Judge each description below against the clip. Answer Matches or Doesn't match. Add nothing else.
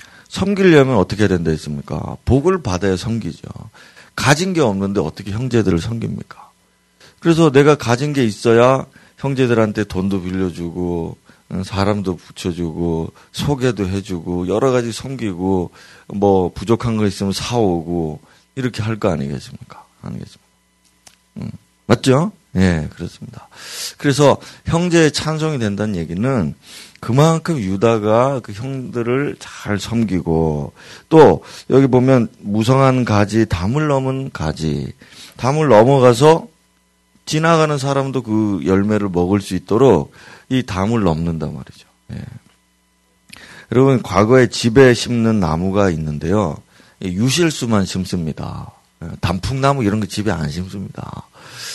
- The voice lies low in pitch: Matches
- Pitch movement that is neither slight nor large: Doesn't match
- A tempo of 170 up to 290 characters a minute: Matches